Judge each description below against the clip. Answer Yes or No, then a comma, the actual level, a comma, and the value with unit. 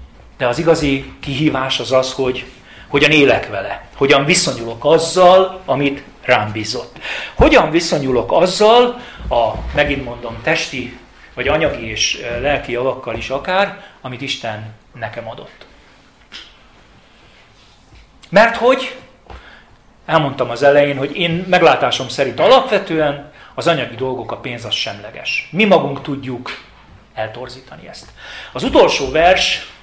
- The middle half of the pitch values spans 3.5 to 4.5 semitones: No, average, 5.1 semitones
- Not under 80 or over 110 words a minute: No, average, 120 wpm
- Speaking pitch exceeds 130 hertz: Yes, medium, 140 Hz